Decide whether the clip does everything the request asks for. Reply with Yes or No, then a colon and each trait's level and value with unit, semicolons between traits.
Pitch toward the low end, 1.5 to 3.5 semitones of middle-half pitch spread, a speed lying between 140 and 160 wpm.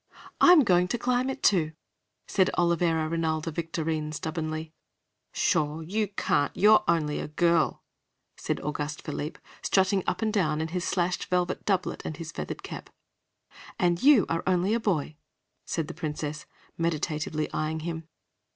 No: medium, 165 Hz; average, 3.0 semitones; average, 150 wpm